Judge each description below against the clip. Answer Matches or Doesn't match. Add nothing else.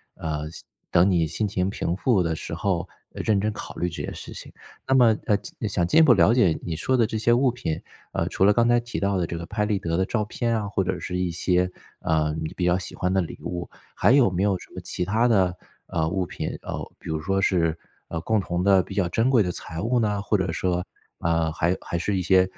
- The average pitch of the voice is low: Matches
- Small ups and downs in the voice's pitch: Doesn't match